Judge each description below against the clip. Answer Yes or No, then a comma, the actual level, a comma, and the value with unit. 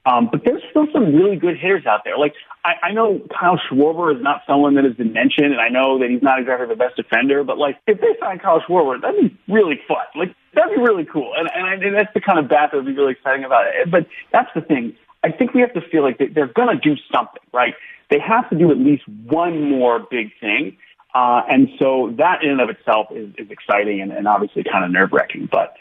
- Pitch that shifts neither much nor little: No, wide, 8.3 semitones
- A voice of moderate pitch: Yes, medium, 150 Hz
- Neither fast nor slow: No, fast, 260 wpm